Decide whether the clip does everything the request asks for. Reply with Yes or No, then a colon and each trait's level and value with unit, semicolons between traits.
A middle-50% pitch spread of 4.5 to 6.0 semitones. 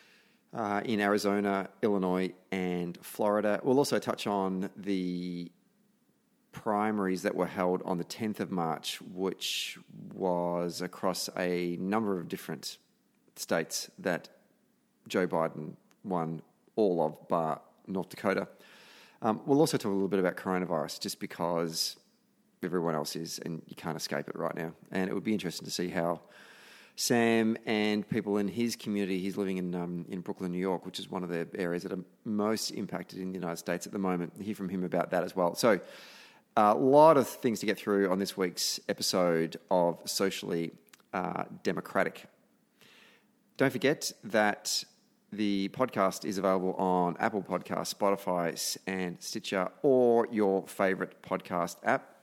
No: average, 2.9 semitones